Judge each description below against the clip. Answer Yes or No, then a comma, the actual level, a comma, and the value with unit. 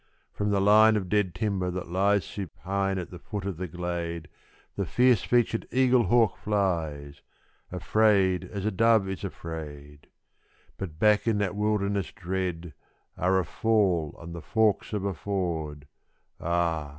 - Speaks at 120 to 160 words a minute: Yes, average, 150 wpm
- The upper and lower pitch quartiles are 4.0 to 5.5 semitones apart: No, average, 3.5 semitones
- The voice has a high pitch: No, very low, 95 Hz